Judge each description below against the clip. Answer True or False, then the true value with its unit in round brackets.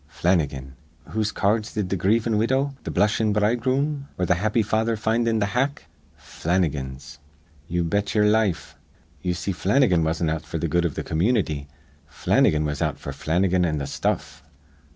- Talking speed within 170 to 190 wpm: True (175 wpm)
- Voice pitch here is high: False (95 Hz)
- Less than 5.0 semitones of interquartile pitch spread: False (5.5 semitones)